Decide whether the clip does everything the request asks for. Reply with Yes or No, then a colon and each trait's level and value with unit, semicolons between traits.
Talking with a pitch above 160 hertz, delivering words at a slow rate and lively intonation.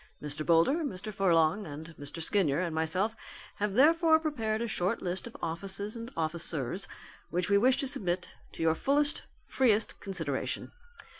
No: high, 190 Hz; average, 155 wpm; wide, 5.8 semitones